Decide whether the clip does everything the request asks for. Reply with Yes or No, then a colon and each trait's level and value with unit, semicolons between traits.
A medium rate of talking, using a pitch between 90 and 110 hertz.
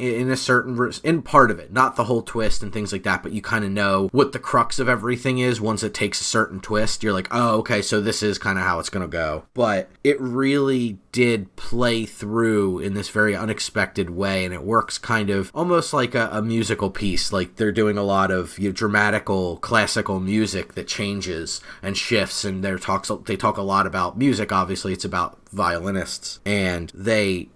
No: fast, 210 wpm; low, 105 Hz